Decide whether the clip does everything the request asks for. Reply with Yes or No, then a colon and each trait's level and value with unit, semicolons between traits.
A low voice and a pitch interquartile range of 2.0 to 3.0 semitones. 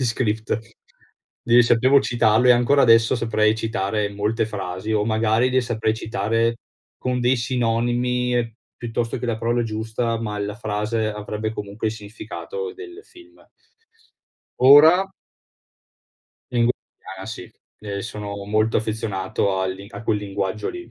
Yes: low, 115 Hz; narrow, 2.4 semitones